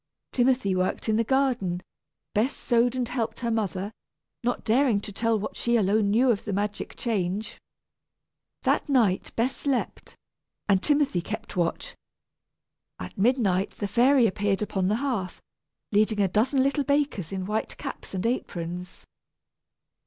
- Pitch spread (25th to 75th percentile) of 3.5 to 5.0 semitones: Yes, average, 4.2 semitones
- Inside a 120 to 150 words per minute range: Yes, average, 145 wpm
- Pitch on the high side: Yes, high, 220 Hz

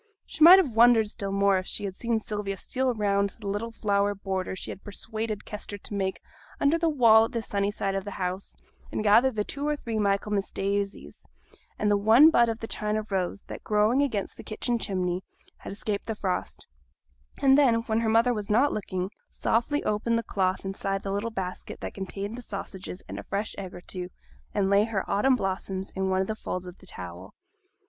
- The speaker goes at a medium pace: No, fast, 215 wpm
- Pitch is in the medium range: No, high, 205 Hz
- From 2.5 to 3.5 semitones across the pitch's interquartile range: Yes, average, 2.8 semitones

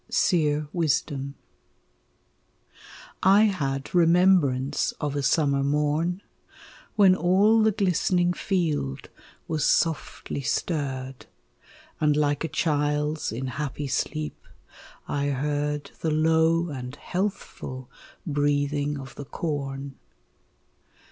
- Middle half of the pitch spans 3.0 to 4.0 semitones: Yes, average, 3.4 semitones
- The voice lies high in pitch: No, medium, 150 Hz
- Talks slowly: Yes, slow, 95 wpm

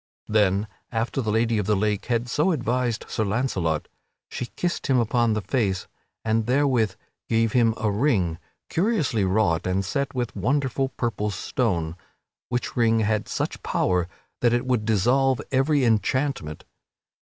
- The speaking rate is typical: Yes, average, 155 wpm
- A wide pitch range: No, average, 3.6 semitones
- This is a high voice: No, low, 115 Hz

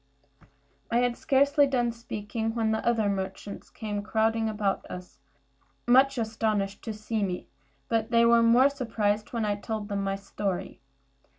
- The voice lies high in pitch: Yes, high, 220 Hz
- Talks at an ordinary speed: Yes, average, 160 wpm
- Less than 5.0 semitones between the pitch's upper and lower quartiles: Yes, narrow, 2.4 semitones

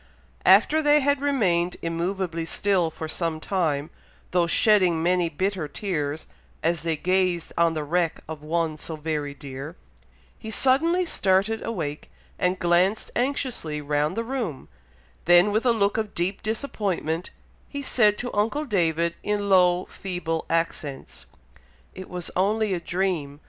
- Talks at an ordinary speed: Yes, average, 145 wpm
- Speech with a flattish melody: No, average, 4.4 semitones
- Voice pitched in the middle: Yes, medium, 180 Hz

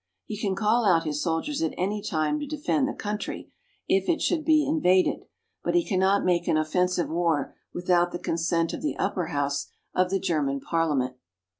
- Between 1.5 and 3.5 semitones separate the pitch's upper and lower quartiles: No, average, 4.7 semitones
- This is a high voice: No, medium, 180 Hz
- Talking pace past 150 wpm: Yes, average, 185 wpm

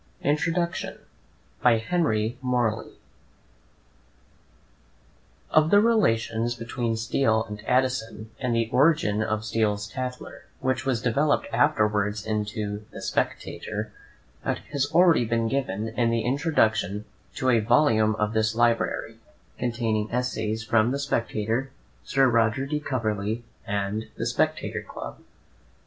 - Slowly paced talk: Yes, slow, 120 wpm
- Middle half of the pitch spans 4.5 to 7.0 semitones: No, average, 3.2 semitones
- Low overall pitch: Yes, low, 115 Hz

